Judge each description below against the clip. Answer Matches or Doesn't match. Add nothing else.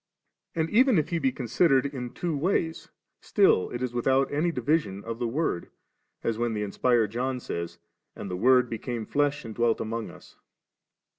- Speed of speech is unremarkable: Matches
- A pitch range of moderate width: Matches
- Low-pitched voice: Matches